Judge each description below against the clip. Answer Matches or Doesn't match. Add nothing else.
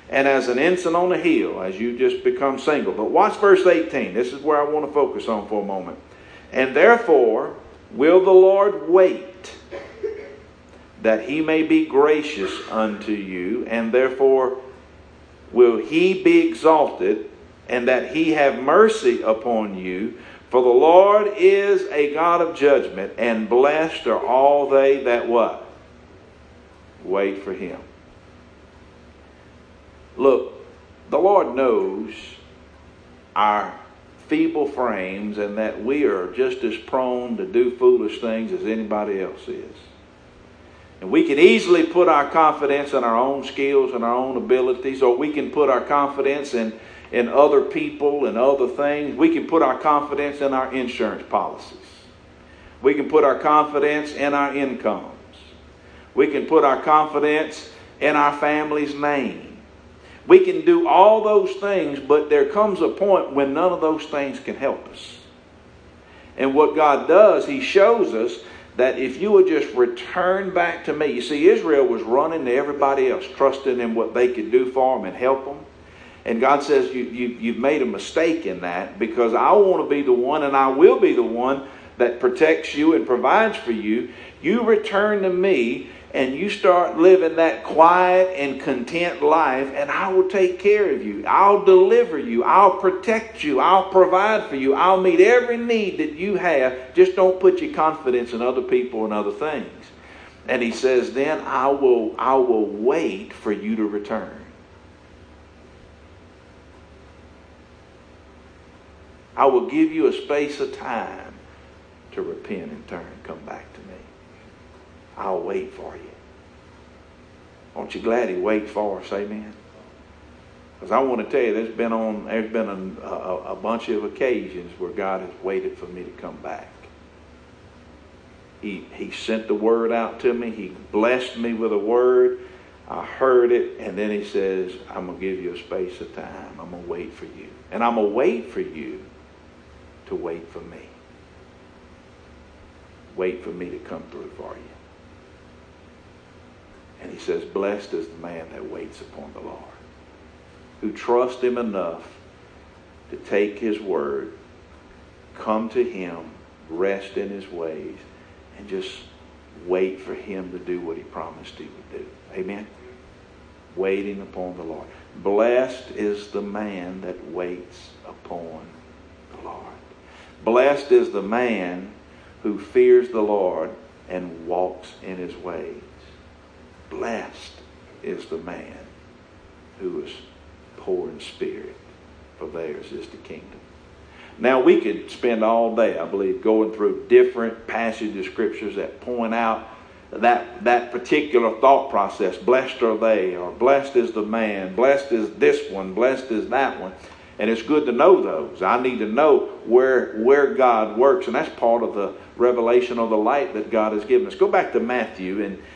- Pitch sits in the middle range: Doesn't match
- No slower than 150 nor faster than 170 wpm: Matches